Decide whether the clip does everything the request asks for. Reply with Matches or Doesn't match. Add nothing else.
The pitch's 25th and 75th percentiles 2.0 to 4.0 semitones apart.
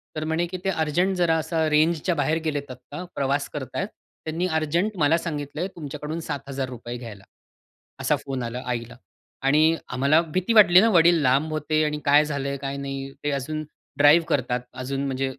Matches